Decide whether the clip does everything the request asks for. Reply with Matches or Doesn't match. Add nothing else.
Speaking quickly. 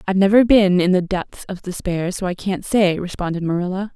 Matches